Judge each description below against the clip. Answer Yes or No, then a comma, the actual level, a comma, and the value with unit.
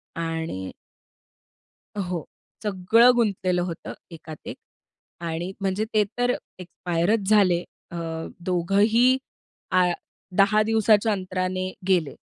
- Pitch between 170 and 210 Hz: Yes, medium, 185 Hz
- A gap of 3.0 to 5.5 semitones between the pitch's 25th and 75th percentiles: Yes, average, 3.5 semitones